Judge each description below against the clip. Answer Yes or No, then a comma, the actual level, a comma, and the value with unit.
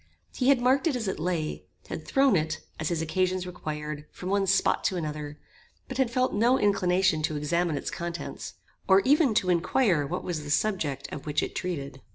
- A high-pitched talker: No, medium, 180 Hz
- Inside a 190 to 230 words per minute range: Yes, average, 200 wpm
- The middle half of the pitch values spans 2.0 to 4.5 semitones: No, average, 5.3 semitones